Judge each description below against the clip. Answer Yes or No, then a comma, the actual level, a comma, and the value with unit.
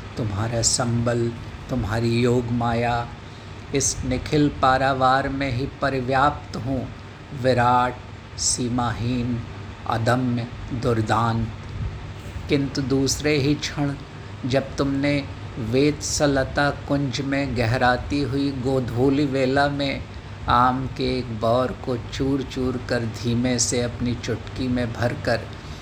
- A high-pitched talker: No, low, 125 Hz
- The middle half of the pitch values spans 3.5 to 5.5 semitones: No, average, 2.8 semitones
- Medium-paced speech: No, slow, 105 wpm